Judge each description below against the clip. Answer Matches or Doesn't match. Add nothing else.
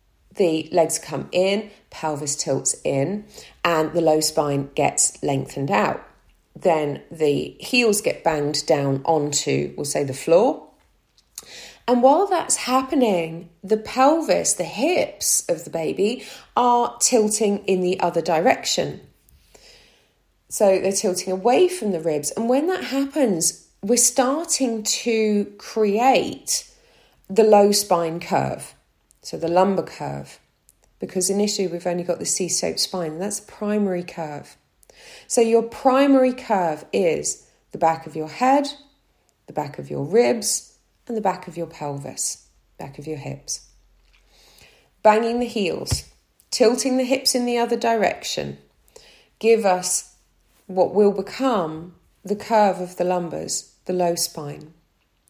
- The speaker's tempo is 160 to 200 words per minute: Doesn't match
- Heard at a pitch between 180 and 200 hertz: Matches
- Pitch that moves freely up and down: Matches